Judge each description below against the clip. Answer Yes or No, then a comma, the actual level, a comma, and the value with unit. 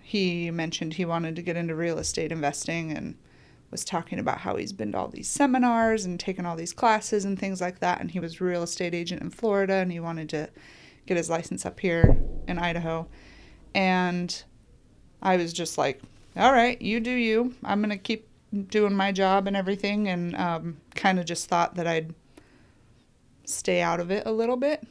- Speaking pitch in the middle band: Yes, medium, 180 Hz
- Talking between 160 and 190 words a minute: No, average, 200 wpm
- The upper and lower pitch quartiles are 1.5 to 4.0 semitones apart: Yes, average, 3.4 semitones